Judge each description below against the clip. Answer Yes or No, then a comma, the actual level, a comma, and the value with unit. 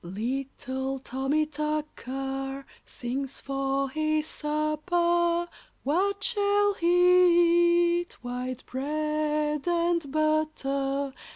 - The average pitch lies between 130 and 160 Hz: No, very high, 305 Hz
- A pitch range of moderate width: Yes, average, 4.1 semitones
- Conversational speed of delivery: No, slow, 85 wpm